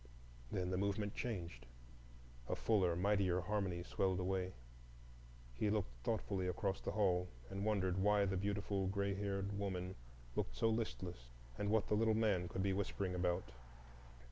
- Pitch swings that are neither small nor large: No, narrow, 2.1 semitones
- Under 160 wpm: Yes, average, 150 wpm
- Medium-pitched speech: No, very low, 95 Hz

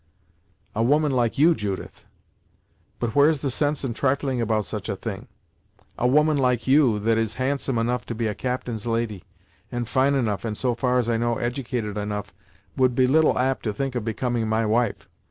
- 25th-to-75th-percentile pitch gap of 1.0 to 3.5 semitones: Yes, average, 3.0 semitones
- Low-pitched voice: Yes, low, 120 Hz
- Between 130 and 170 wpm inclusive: No, average, 190 wpm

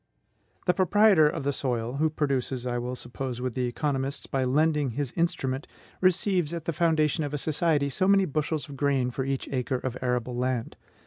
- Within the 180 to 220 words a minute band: Yes, average, 190 wpm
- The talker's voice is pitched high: No, medium, 140 Hz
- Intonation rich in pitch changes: No, average, 3.8 semitones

